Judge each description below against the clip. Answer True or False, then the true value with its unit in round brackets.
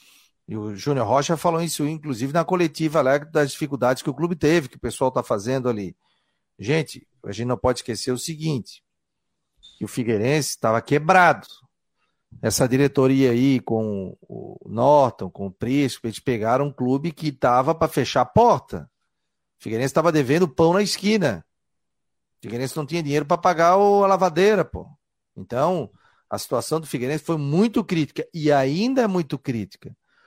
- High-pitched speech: False (145 Hz)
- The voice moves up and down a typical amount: True (4.8 semitones)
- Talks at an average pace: True (165 wpm)